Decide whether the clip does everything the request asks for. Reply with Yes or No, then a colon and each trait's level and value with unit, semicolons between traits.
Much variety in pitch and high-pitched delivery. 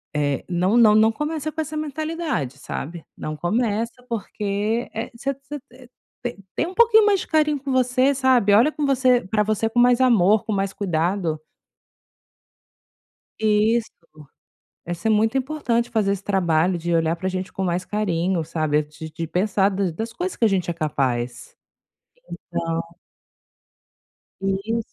Yes: wide, 6.5 semitones; high, 210 Hz